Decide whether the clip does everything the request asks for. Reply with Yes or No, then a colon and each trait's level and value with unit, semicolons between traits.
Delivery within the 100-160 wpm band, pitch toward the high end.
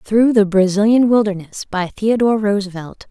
Yes: slow, 135 wpm; high, 205 Hz